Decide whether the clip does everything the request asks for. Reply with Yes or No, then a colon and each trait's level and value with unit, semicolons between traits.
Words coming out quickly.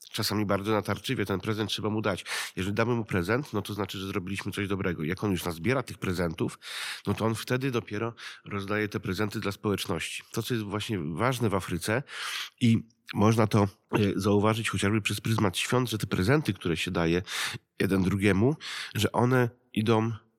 Yes: fast, 180 wpm